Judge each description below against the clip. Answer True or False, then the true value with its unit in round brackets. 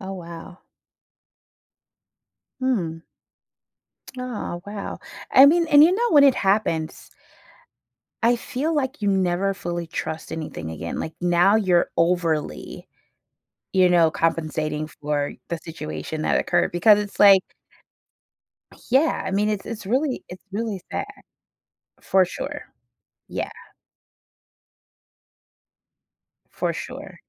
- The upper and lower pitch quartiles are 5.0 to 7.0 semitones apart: True (5.4 semitones)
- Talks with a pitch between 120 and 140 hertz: False (190 Hz)